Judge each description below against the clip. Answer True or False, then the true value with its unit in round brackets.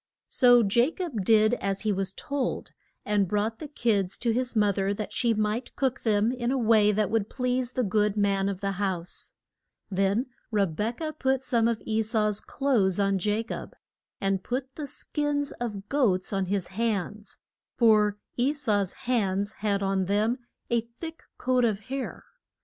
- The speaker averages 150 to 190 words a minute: True (180 wpm)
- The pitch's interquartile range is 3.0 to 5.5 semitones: True (3.7 semitones)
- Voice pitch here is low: False (215 Hz)